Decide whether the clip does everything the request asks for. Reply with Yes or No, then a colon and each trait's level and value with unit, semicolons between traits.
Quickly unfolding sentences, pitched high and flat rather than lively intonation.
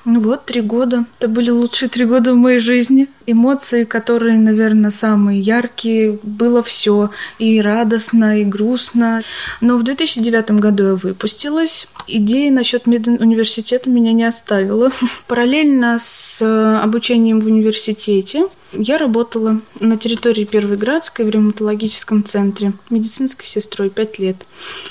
No: average, 130 wpm; high, 230 Hz; narrow, 2.3 semitones